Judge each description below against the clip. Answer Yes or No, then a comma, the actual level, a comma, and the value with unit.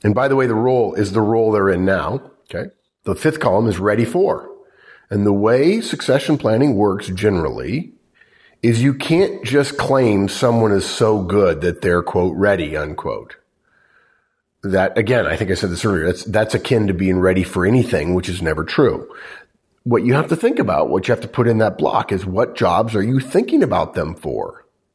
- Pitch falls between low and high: No, low, 110 Hz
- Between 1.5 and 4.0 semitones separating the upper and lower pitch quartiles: No, average, 4.9 semitones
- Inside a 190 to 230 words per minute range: Yes, average, 200 wpm